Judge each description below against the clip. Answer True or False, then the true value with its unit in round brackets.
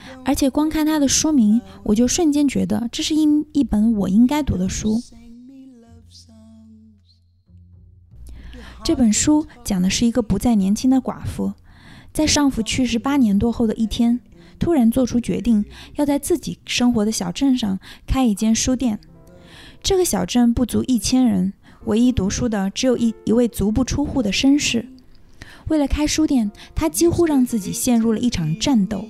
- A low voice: False (235 Hz)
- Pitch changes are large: False (4.8 semitones)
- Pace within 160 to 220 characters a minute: False (240 characters per minute)